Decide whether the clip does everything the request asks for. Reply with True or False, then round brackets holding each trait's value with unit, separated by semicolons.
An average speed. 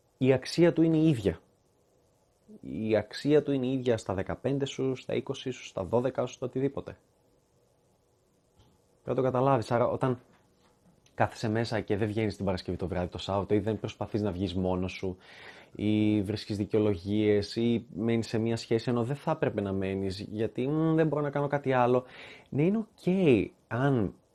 False (180 wpm)